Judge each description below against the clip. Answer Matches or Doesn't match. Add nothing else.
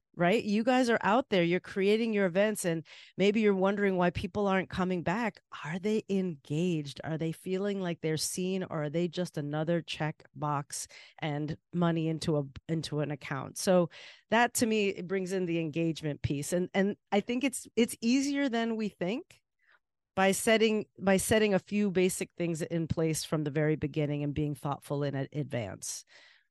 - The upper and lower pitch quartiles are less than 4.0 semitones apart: Doesn't match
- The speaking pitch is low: Doesn't match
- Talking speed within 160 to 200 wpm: Matches